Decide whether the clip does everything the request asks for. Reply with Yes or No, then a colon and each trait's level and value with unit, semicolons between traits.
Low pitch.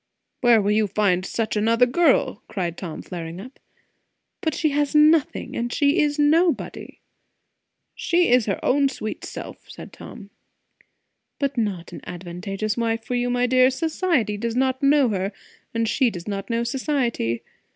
No: high, 235 Hz